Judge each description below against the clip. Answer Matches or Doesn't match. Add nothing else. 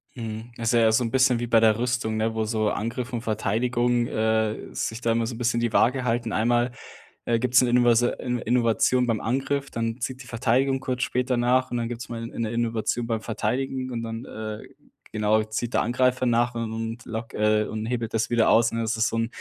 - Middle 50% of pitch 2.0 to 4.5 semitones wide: Doesn't match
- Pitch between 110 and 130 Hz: Matches